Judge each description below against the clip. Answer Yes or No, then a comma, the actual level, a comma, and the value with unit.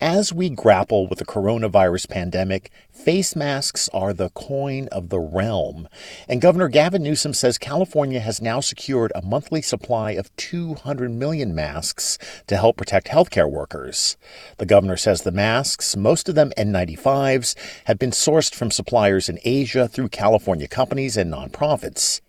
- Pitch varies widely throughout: Yes, wide, 6.5 semitones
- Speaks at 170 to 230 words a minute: No, average, 155 wpm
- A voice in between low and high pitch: No, low, 125 Hz